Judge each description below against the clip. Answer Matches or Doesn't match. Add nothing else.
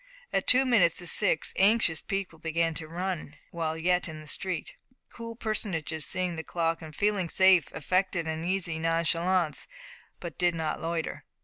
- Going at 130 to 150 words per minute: Doesn't match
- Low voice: Doesn't match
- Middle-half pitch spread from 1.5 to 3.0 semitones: Matches